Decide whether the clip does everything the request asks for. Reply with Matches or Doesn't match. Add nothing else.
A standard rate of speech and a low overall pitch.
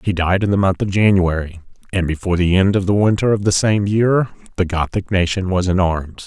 Doesn't match